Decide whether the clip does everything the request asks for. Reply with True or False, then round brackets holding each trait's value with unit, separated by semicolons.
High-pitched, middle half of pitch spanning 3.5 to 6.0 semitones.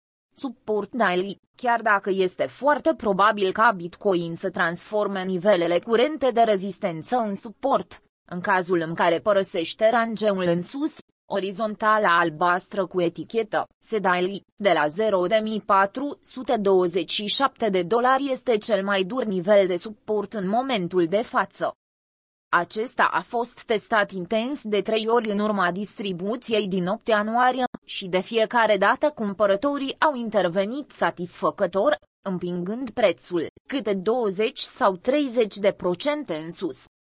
True (210 Hz; 3.9 semitones)